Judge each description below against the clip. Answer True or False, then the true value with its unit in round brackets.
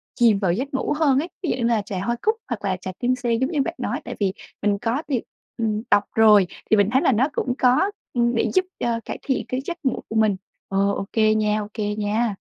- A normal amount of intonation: True (3.8 semitones)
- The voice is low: False (230 Hz)